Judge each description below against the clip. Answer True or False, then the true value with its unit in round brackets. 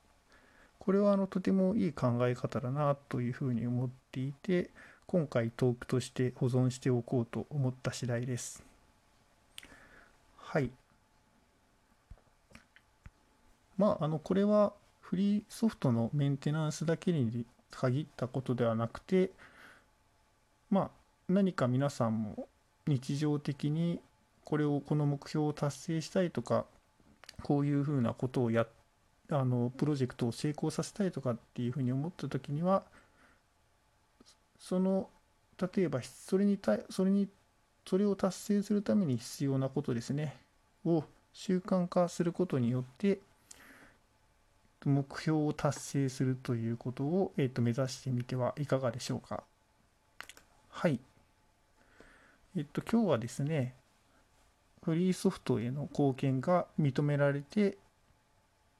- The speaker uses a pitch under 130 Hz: False (140 Hz)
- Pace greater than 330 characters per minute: False (260 characters per minute)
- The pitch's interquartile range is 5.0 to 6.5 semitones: True (5.9 semitones)